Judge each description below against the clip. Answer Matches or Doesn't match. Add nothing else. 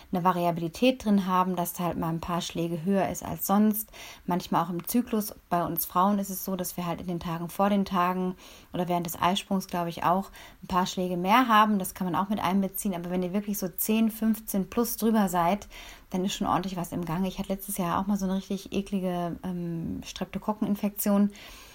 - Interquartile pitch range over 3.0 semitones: Doesn't match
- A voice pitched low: Doesn't match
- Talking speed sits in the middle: Doesn't match